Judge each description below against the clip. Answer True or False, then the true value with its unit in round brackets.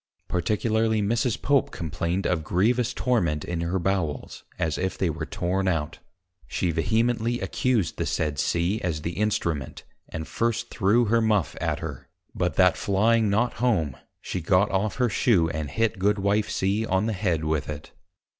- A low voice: True (95 Hz)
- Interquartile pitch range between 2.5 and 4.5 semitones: False (5.0 semitones)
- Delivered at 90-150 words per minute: False (165 wpm)